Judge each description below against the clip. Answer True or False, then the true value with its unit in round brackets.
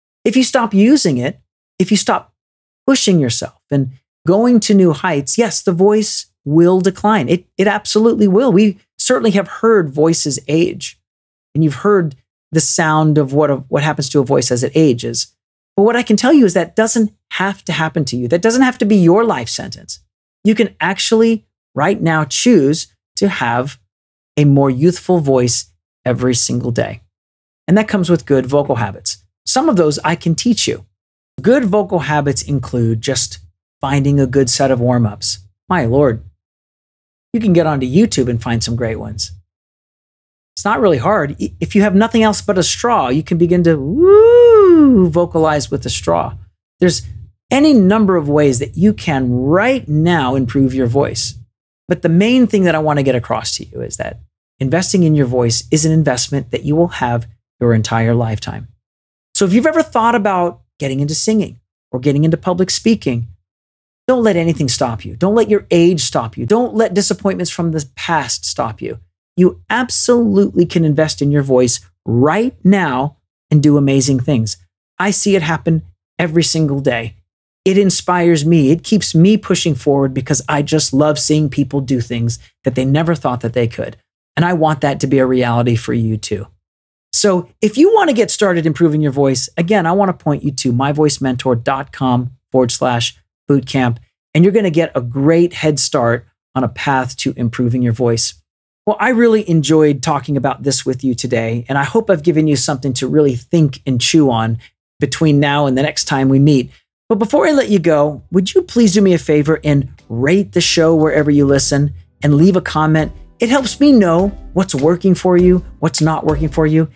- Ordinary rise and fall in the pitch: False (6.8 semitones)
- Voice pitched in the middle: True (150 Hz)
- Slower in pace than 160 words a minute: False (190 wpm)